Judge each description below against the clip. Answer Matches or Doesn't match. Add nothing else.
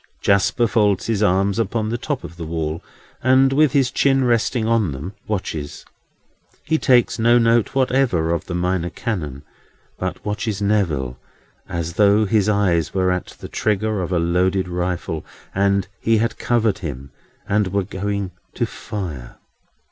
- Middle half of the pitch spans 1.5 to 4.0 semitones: Doesn't match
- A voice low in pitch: Matches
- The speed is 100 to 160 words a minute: Matches